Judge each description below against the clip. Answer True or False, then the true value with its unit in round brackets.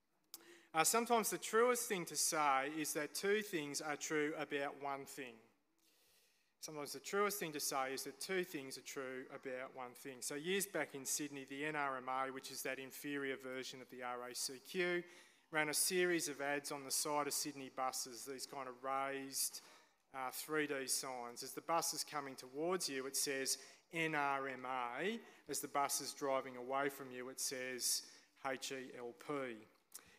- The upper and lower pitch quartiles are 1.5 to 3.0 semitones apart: True (2.4 semitones)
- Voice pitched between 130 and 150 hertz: True (140 Hz)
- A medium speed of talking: True (170 wpm)